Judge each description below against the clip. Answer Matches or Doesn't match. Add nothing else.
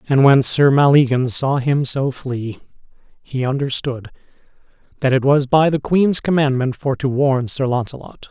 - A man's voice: Matches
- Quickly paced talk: Doesn't match